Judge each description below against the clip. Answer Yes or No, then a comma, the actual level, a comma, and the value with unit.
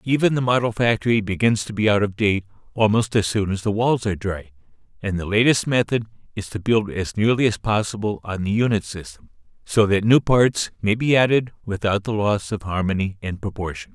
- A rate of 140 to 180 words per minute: No, average, 200 wpm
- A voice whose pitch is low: Yes, low, 105 Hz